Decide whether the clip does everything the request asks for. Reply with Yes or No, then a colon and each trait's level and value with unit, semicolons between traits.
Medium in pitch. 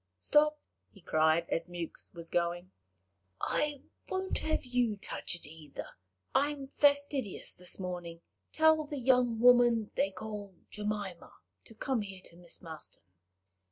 No: high, 210 Hz